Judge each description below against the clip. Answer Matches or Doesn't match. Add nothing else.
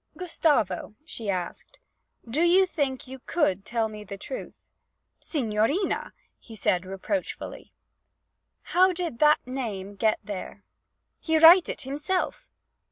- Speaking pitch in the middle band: Doesn't match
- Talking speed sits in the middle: Doesn't match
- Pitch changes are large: Matches